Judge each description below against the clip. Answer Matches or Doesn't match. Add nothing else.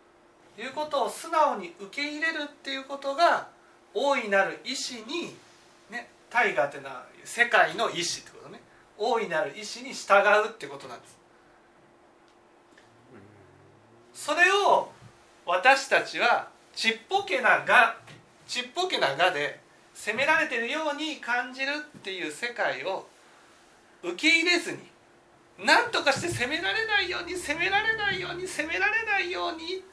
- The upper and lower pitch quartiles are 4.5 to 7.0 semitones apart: Doesn't match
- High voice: Matches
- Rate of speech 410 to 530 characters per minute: Doesn't match